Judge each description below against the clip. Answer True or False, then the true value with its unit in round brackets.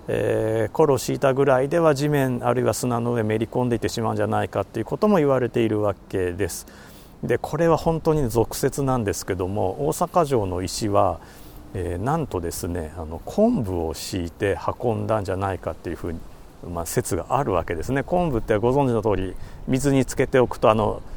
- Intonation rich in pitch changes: True (6.0 semitones)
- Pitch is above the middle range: False (110 Hz)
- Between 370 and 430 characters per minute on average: True (395 characters per minute)